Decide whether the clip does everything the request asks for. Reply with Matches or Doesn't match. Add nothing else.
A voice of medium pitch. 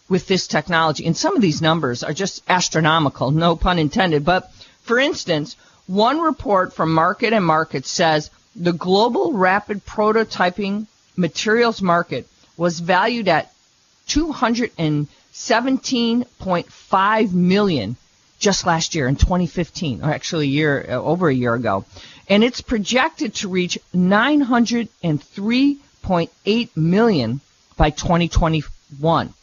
Matches